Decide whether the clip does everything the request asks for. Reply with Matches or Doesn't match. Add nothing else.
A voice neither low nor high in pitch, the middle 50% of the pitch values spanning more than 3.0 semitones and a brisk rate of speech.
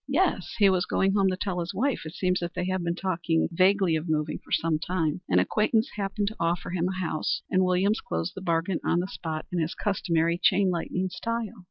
Doesn't match